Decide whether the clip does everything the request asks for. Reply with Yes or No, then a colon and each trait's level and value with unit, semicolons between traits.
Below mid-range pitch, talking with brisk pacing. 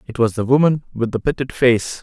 Yes: low, 125 Hz; fast, 235 wpm